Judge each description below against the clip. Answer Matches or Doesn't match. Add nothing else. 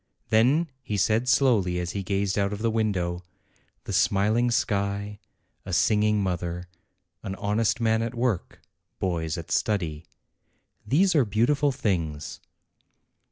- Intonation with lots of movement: Doesn't match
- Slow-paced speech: Matches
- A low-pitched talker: Matches